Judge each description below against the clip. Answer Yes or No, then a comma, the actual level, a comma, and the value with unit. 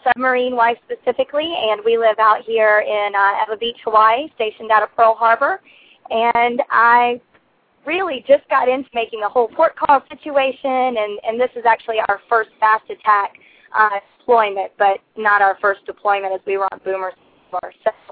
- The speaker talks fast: No, average, 180 wpm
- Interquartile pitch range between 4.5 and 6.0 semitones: No, average, 3.5 semitones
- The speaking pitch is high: Yes, high, 230 Hz